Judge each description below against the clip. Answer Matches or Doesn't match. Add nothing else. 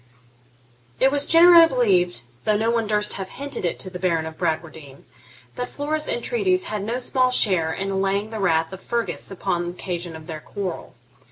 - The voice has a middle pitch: Doesn't match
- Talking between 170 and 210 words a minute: Matches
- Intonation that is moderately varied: Doesn't match